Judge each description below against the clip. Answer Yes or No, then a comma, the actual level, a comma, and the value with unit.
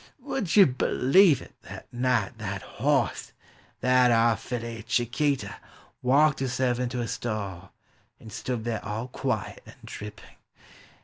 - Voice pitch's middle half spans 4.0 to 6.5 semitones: No, average, 2.8 semitones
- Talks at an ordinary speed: Yes, average, 145 wpm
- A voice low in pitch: Yes, low, 120 Hz